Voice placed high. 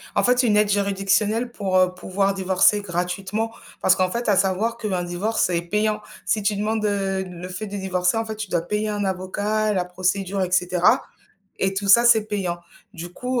Yes: high, 195 Hz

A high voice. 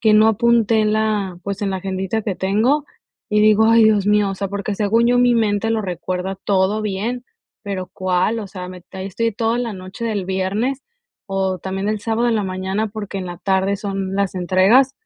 Yes: high, 200 Hz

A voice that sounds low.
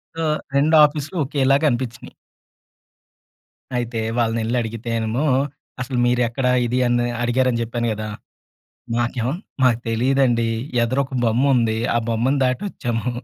Yes: low, 120 Hz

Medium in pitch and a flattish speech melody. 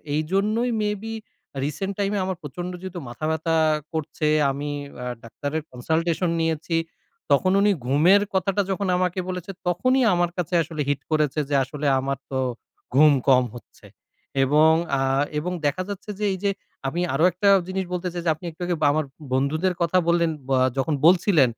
No: medium, 165 Hz; average, 4.0 semitones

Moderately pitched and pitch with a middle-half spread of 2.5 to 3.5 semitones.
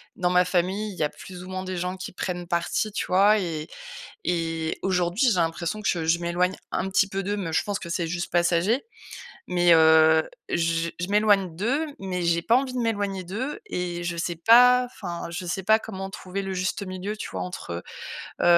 Yes: medium, 180 Hz; average, 3.0 semitones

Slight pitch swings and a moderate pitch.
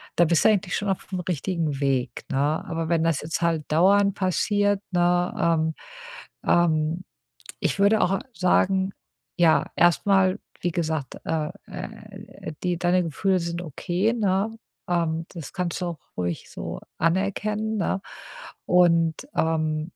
No: average, 3.1 semitones; medium, 175 Hz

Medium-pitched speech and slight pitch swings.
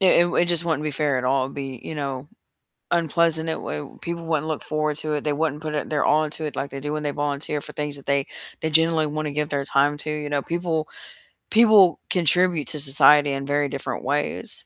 Yes: medium, 150 Hz; narrow, 2.1 semitones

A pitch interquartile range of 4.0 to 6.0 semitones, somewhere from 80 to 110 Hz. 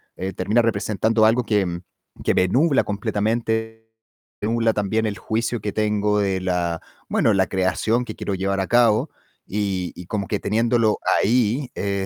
No: narrow, 2.6 semitones; low, 105 Hz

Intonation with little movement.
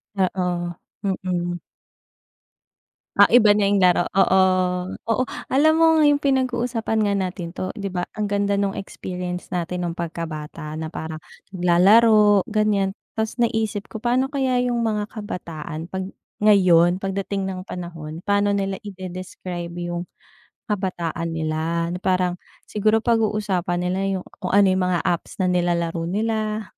No: average, 3.3 semitones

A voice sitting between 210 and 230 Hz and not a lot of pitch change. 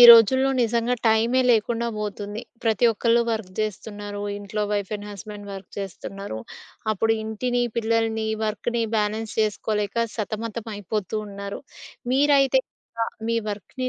Yes: high, 220 Hz; narrow, 2.1 semitones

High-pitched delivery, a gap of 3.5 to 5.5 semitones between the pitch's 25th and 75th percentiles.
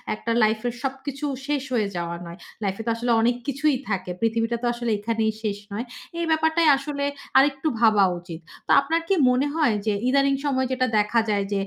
Yes: high, 240 Hz; average, 4.6 semitones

